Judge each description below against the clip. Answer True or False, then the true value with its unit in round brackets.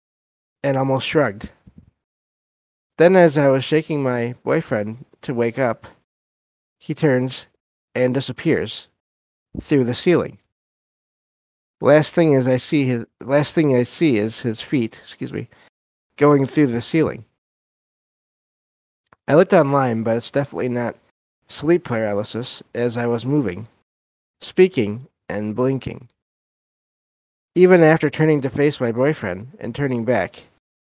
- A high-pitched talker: False (130 Hz)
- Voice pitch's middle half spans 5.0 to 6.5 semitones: False (4.4 semitones)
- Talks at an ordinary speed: False (125 wpm)